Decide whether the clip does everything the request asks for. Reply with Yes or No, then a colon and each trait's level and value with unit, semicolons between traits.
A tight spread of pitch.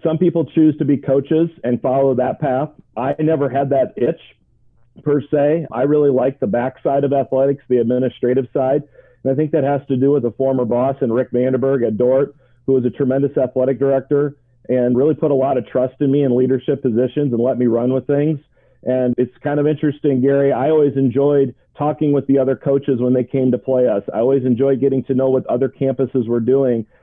Yes: narrow, 2.0 semitones